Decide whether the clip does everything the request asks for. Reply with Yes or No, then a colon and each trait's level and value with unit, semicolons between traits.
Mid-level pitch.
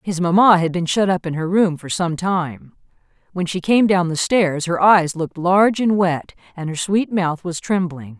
Yes: medium, 175 Hz